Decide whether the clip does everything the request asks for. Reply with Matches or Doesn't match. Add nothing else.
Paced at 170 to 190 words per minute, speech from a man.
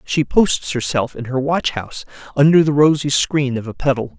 Doesn't match